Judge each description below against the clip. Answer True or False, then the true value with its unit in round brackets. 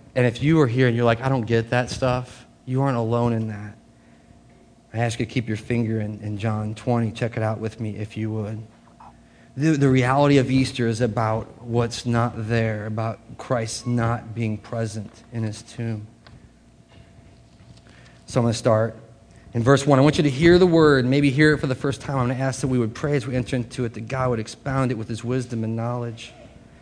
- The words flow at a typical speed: False (225 wpm)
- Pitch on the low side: True (120 Hz)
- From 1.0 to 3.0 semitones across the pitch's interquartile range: True (2.6 semitones)